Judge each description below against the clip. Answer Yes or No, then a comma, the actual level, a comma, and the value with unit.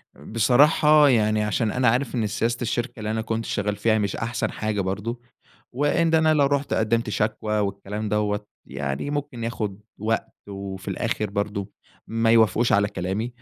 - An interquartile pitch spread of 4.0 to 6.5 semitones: No, average, 2.7 semitones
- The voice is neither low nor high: No, low, 110 Hz